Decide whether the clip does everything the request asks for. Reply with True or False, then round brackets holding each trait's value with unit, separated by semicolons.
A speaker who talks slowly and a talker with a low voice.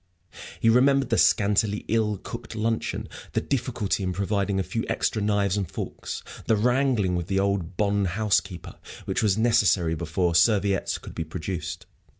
False (155 wpm; 100 Hz)